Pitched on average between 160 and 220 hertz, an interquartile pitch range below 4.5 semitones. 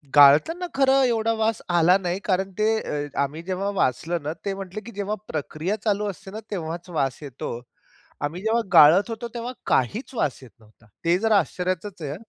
No: medium, 185 Hz; wide, 5.5 semitones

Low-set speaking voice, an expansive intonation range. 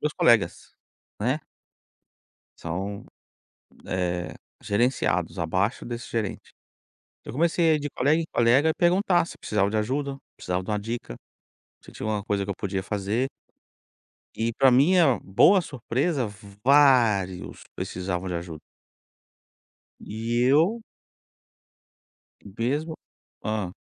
Yes: low, 115 Hz; wide, 6.4 semitones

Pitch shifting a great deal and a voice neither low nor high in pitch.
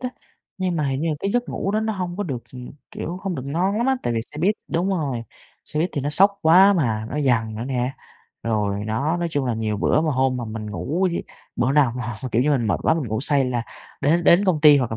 Yes: wide, 6.6 semitones; medium, 145 Hz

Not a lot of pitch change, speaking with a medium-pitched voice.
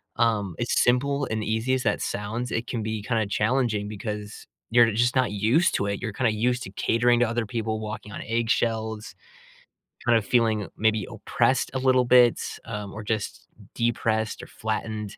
No: narrow, 2.2 semitones; low, 110 Hz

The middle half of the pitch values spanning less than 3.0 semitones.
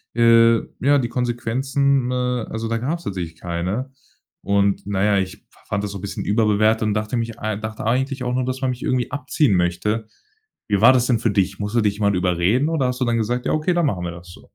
No: average, 4.0 semitones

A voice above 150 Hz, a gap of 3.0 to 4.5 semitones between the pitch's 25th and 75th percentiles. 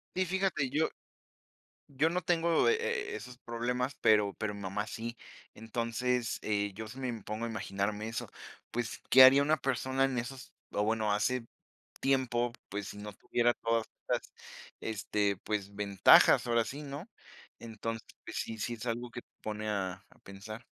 No: low, 115 Hz; average, 3.3 semitones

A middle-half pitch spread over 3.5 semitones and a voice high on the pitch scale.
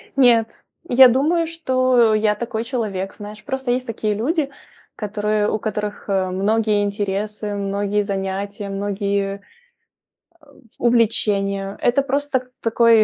No: average, 3.2 semitones; high, 215 Hz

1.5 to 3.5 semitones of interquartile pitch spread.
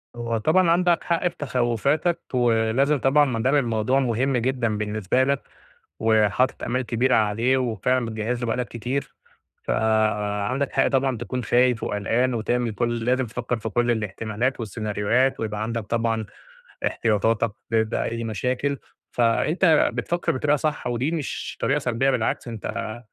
Yes: average, 2.9 semitones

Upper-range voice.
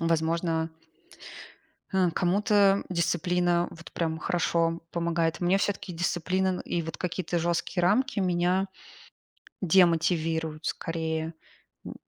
No: medium, 175 Hz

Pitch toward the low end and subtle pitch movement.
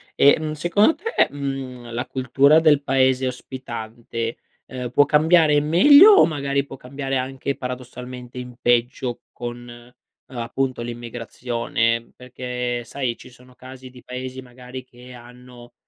Yes: low, 125 Hz; narrow, 2.2 semitones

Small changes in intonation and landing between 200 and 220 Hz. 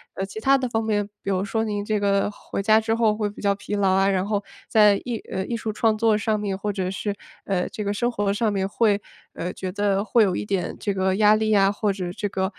Yes: narrow, 1.8 semitones; high, 205 Hz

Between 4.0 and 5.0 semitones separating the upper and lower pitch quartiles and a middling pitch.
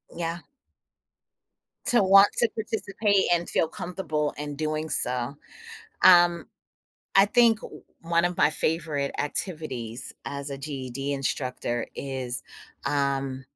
Yes: average, 4.3 semitones; medium, 155 Hz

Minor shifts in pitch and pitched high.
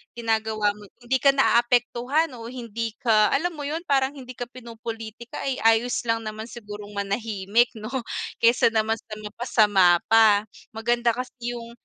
Yes: narrow, 2.2 semitones; high, 230 Hz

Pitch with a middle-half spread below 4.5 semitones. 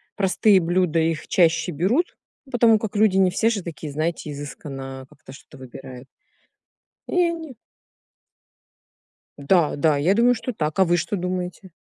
No: average, 5.3 semitones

